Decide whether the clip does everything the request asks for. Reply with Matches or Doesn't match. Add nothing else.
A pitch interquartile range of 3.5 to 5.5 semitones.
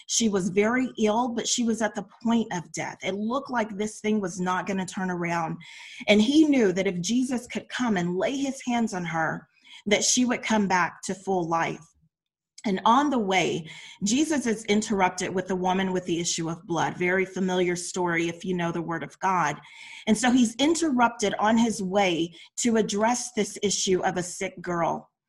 Matches